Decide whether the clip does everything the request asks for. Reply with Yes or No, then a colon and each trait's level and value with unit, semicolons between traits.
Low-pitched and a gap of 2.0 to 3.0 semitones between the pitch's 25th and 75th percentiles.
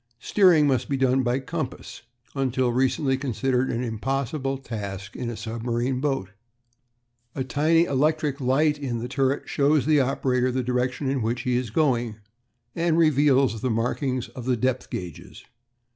Yes: low, 130 Hz; narrow, 2.6 semitones